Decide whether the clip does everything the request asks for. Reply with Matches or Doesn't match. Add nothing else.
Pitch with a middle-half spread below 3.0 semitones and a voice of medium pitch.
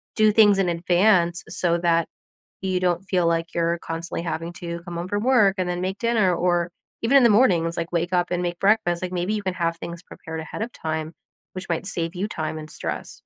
Matches